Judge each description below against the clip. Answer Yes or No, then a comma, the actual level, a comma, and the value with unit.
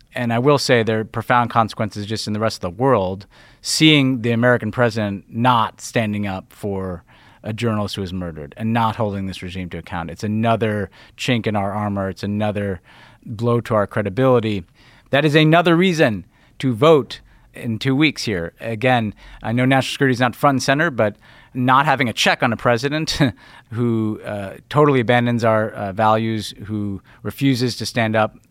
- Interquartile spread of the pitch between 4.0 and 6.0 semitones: No, average, 3.5 semitones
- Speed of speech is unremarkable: Yes, average, 185 wpm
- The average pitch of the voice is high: No, low, 115 Hz